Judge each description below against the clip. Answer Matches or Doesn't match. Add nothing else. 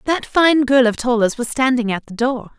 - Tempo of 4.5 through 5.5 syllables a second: Matches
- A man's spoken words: Doesn't match